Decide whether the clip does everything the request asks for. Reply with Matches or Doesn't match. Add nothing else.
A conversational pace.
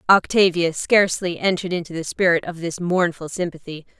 Matches